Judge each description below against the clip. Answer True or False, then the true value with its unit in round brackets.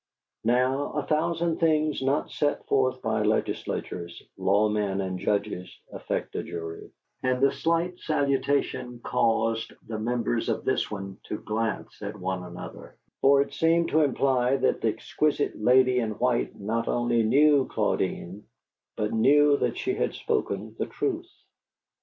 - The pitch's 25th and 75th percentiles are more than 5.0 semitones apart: True (5.4 semitones)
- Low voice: True (125 Hz)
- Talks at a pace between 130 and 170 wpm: True (145 wpm)